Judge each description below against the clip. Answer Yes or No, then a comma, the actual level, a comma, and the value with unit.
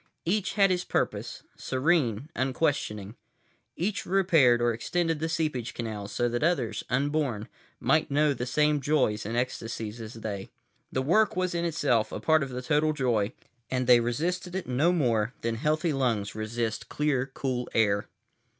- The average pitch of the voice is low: Yes, low, 130 Hz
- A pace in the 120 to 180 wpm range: Yes, average, 160 wpm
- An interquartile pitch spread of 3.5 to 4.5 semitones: No, wide, 5.4 semitones